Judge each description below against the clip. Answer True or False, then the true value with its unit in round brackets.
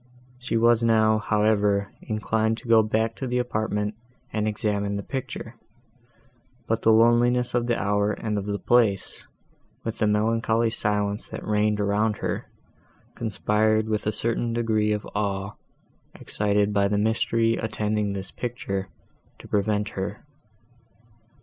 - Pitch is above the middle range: False (110 Hz)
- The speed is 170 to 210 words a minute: False (140 wpm)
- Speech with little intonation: True (1.7 semitones)